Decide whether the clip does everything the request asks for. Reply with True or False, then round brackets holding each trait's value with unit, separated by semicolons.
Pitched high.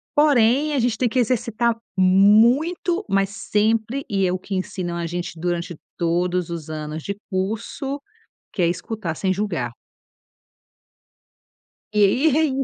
True (205 Hz)